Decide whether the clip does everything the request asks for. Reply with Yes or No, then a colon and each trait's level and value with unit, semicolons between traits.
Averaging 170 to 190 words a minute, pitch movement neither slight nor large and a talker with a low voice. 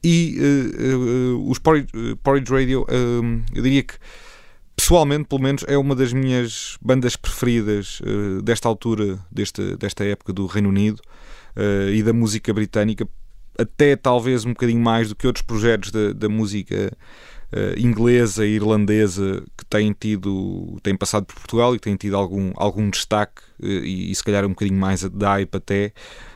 Yes: average, 175 wpm; average, 3.4 semitones; low, 110 Hz